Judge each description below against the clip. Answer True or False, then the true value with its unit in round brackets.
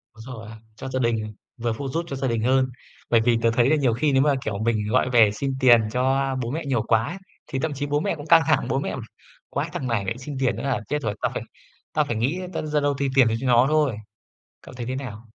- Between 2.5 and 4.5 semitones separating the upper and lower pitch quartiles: True (3.3 semitones)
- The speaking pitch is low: True (130 Hz)